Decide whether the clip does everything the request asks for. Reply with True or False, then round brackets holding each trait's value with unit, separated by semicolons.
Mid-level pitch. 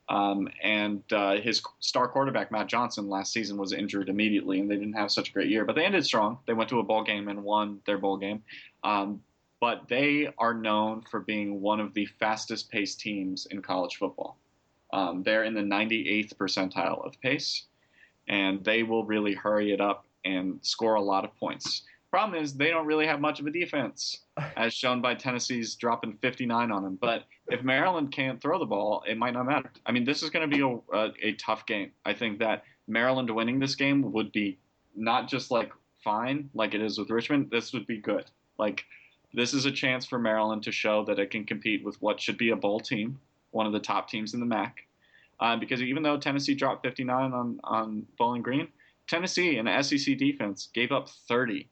False (110 Hz)